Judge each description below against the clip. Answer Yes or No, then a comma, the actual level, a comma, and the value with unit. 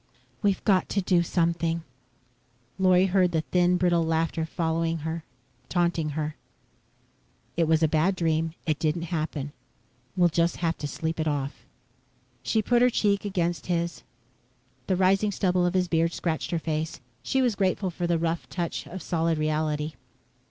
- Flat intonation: Yes, narrow, 2.2 semitones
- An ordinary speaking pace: Yes, average, 165 wpm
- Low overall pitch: No, medium, 170 Hz